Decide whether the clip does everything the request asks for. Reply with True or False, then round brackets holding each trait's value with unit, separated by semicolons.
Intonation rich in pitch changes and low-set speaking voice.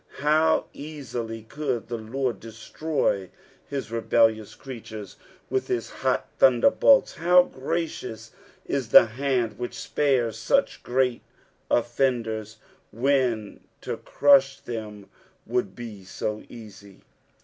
False (3.7 semitones; 120 Hz)